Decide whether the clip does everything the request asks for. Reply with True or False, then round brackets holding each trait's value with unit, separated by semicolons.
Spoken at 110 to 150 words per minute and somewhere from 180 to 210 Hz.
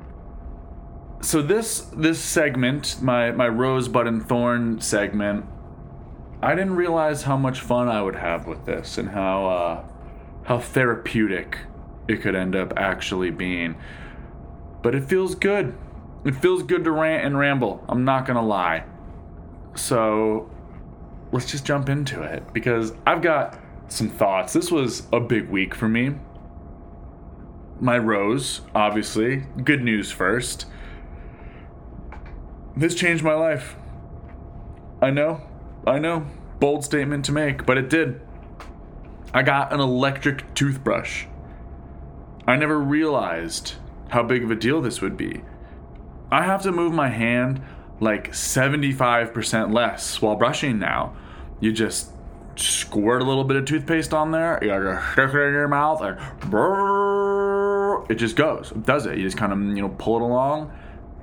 False (140 wpm; 115 Hz)